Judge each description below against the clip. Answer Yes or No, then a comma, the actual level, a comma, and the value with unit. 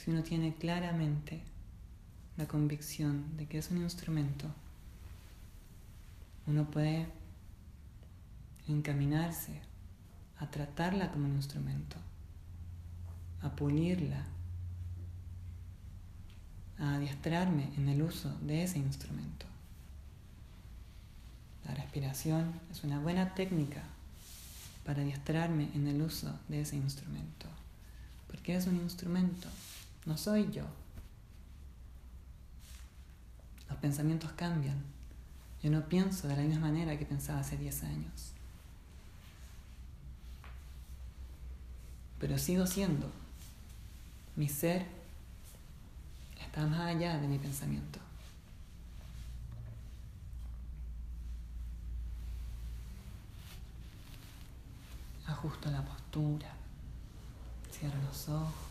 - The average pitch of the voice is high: No, very low, 95 Hz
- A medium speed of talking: No, slow, 85 wpm